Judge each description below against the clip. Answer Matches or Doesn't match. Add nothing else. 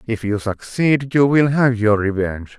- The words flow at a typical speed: Matches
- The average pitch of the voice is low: Matches